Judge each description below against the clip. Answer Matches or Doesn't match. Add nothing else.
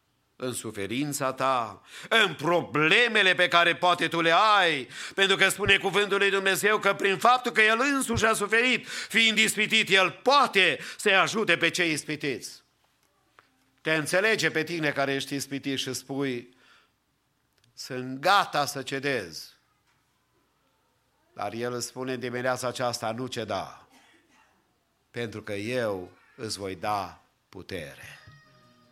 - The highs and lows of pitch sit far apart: Matches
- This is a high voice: Doesn't match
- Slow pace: Matches